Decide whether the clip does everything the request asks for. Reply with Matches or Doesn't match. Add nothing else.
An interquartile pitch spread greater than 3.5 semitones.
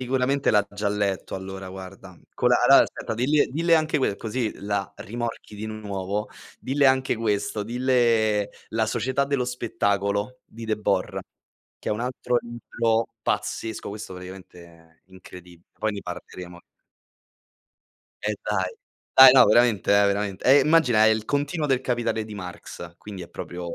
Matches